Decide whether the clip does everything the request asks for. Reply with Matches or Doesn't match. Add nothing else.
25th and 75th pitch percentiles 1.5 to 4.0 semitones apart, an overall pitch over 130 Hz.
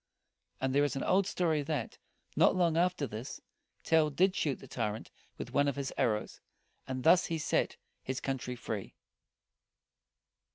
Doesn't match